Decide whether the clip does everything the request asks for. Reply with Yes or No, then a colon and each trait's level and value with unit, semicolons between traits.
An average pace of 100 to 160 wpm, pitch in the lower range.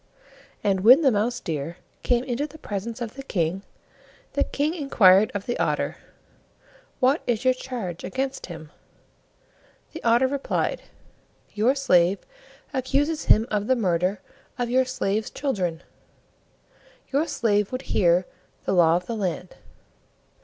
No: average, 140 wpm; high, 225 Hz